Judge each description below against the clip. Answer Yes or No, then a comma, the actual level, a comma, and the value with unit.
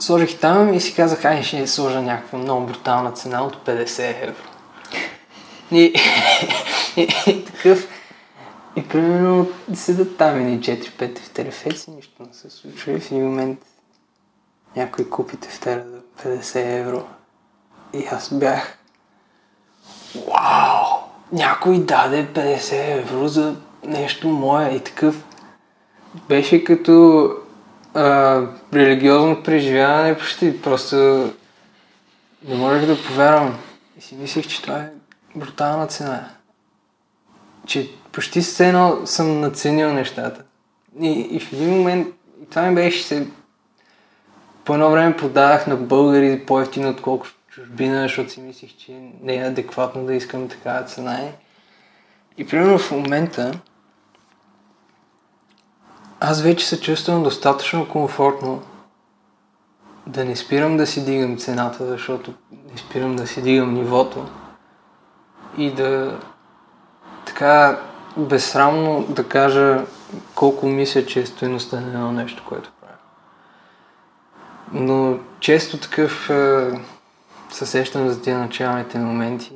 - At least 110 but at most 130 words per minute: Yes, average, 120 wpm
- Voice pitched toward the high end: No, medium, 140 Hz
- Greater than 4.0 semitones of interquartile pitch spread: No, average, 3.3 semitones